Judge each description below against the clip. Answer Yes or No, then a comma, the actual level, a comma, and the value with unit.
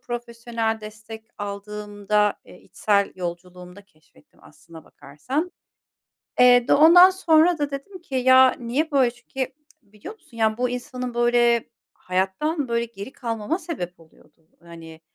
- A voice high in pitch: Yes, high, 235 Hz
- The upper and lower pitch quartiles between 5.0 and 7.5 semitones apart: No, average, 4.6 semitones